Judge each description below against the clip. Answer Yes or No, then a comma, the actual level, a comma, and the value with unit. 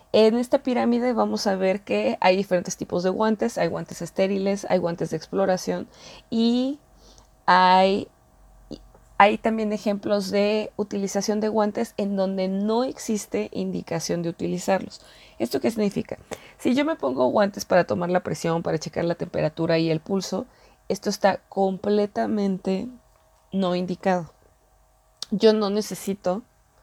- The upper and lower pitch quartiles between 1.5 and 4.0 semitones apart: Yes, average, 2.9 semitones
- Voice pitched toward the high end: Yes, high, 195 Hz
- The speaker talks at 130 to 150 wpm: Yes, average, 140 wpm